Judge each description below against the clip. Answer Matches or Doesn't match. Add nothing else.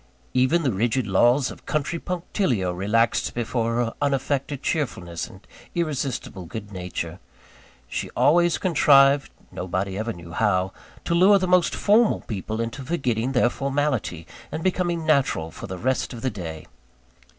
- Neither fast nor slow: Matches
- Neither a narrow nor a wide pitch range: Doesn't match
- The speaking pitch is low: Matches